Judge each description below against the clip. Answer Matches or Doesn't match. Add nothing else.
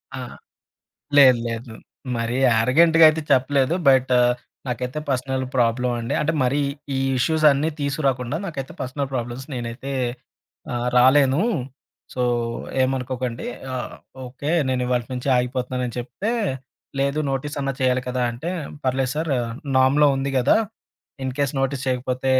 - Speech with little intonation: Matches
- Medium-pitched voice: Doesn't match